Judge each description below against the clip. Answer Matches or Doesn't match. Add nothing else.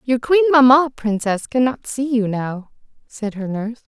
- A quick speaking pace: Doesn't match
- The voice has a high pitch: Matches